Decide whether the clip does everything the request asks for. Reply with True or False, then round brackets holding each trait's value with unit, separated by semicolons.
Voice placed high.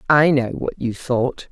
False (130 Hz)